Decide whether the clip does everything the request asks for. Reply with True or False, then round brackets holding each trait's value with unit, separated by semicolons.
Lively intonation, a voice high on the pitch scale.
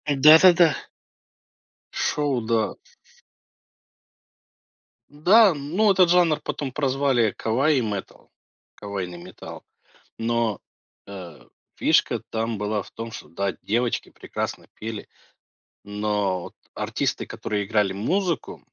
False (6.4 semitones; 115 Hz)